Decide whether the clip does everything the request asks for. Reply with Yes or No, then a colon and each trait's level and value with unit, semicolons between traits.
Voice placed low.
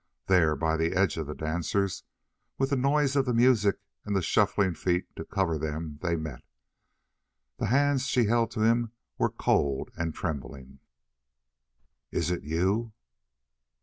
Yes: very low, 95 Hz